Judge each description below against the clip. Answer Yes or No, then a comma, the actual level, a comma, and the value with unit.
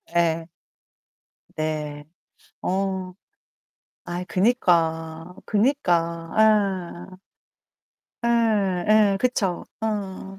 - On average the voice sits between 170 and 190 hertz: Yes, medium, 185 Hz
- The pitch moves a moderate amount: Yes, average, 3.7 semitones